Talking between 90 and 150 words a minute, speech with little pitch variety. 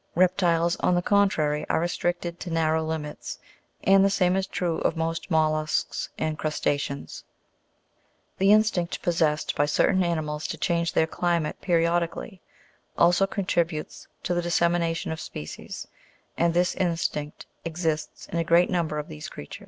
Yes: average, 145 wpm; narrow, 2.1 semitones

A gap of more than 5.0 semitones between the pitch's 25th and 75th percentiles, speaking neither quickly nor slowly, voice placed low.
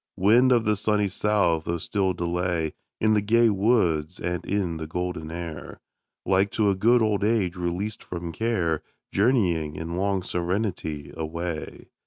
No: average, 3.9 semitones; average, 155 wpm; very low, 90 Hz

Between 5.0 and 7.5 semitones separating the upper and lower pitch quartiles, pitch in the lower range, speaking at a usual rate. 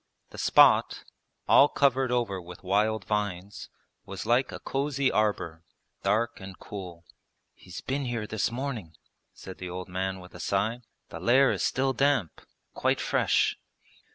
Yes: wide, 5.4 semitones; low, 105 Hz; average, 150 wpm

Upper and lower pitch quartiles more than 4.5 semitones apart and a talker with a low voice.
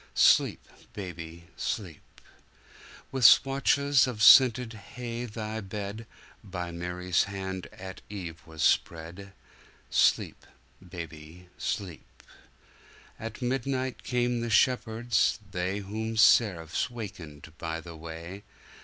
Yes: average, 5.1 semitones; low, 100 Hz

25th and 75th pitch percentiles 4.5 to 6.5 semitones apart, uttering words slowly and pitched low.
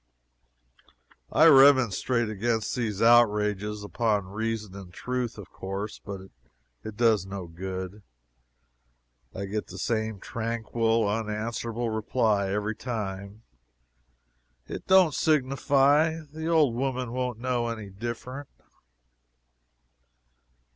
No: average, 3.4 semitones; slow, 100 wpm; low, 110 Hz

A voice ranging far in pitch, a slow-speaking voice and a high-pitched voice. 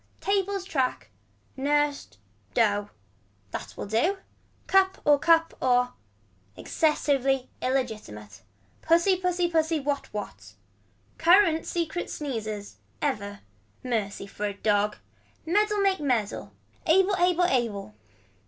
Yes: wide, 8.1 semitones; slow, 105 wpm; very high, 285 Hz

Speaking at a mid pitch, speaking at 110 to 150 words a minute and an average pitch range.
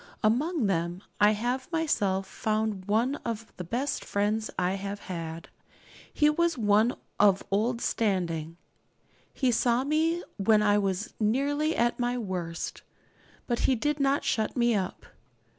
No: high, 220 Hz; average, 140 wpm; average, 4.7 semitones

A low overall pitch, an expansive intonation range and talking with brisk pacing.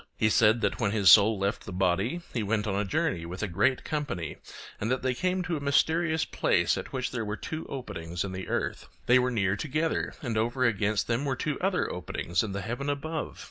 Yes: low, 115 Hz; wide, 6.1 semitones; fast, 225 wpm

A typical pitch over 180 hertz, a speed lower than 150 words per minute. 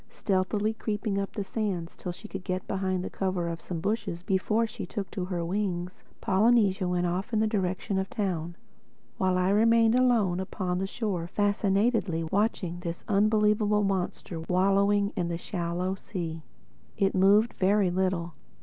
No: high, 190 Hz; average, 165 wpm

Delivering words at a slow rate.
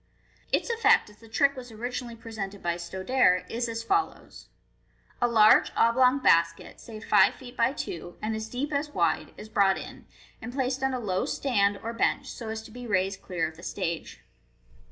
No: average, 195 wpm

